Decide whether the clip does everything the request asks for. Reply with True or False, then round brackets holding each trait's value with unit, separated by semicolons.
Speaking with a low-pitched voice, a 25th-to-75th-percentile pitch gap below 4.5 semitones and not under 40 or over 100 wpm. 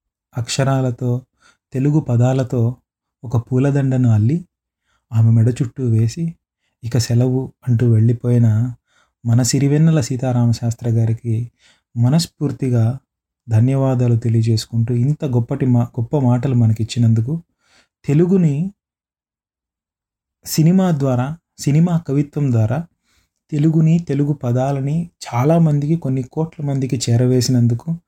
True (125 Hz; 3.6 semitones; 90 wpm)